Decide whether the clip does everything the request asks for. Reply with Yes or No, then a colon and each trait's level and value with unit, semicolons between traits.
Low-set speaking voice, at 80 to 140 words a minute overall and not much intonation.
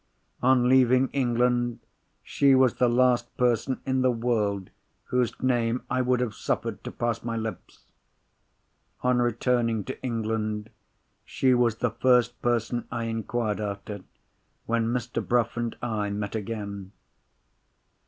Yes: low, 120 Hz; slow, 135 wpm; narrow, 2.0 semitones